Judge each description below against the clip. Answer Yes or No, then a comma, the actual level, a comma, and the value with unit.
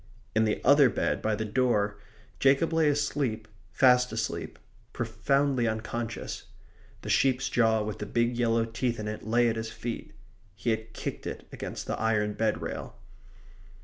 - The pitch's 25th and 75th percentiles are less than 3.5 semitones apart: Yes, narrow, 2.4 semitones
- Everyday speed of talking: Yes, average, 160 wpm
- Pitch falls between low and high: No, low, 115 Hz